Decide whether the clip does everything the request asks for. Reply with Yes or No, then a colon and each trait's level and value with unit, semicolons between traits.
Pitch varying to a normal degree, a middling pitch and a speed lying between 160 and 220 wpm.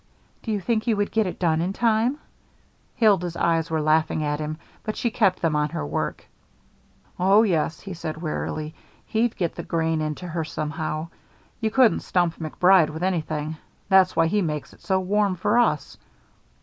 Yes: average, 4.6 semitones; medium, 170 Hz; average, 180 wpm